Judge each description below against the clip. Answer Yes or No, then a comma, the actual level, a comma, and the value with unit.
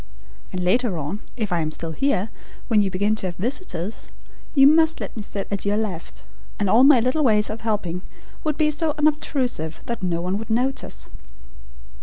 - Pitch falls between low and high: No, high, 215 Hz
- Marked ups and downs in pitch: Yes, wide, 6.6 semitones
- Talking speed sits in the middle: Yes, average, 190 wpm